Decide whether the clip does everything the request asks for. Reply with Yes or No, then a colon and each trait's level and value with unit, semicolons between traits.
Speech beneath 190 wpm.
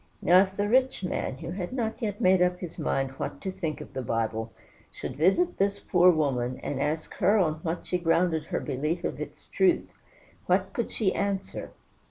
No: average, 200 wpm